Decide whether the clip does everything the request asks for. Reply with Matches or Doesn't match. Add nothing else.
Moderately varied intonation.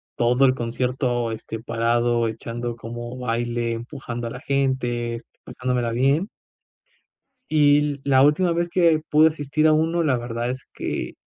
Matches